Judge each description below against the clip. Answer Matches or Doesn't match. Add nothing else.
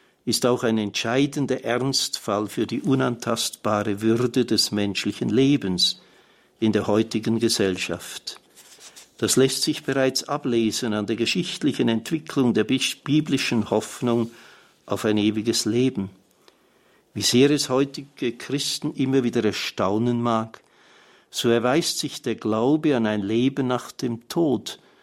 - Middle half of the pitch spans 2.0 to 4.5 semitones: Matches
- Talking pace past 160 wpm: Doesn't match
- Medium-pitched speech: Doesn't match